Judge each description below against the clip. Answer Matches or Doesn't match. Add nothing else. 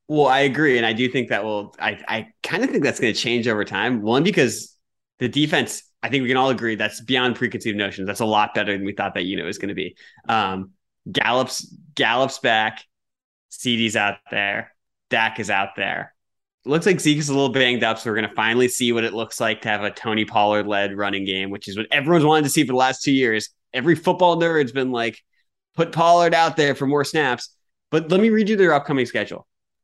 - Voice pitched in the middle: Doesn't match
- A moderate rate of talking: Doesn't match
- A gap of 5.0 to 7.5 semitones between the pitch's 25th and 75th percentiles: Matches